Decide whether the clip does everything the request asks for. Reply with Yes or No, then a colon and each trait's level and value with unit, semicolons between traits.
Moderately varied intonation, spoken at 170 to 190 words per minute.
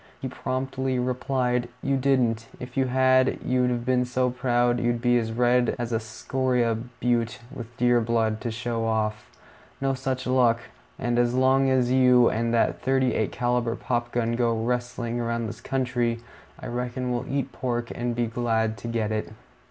No: narrow, 1.6 semitones; average, 175 wpm